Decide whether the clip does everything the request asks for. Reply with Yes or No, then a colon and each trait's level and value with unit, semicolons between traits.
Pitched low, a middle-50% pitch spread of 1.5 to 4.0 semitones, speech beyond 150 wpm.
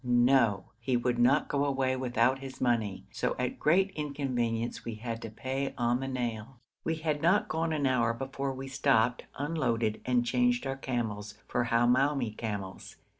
Yes: low, 125 Hz; average, 2.7 semitones; average, 170 wpm